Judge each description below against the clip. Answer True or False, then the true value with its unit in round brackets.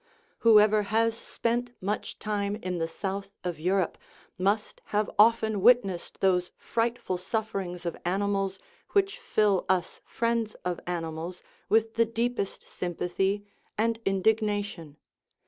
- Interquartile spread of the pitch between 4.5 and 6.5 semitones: False (3.5 semitones)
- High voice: True (205 Hz)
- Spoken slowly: True (125 wpm)